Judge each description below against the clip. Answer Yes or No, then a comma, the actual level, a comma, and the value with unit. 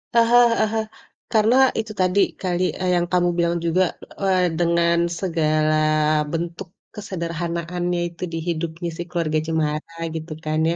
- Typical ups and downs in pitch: No, narrow, 1.9 semitones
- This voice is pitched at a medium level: Yes, medium, 170 Hz